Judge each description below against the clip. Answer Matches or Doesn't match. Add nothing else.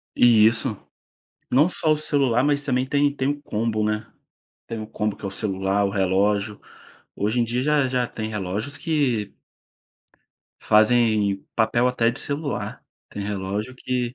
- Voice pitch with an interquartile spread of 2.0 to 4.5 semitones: Matches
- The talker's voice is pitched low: Matches